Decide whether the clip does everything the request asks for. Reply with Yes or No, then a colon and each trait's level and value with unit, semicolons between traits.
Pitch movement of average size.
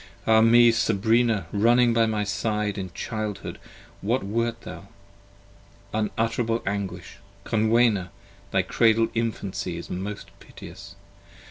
No: narrow, 2.2 semitones